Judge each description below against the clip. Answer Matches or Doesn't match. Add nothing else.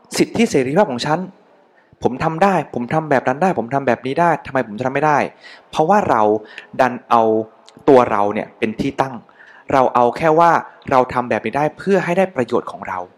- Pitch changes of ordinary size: Doesn't match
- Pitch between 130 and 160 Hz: Matches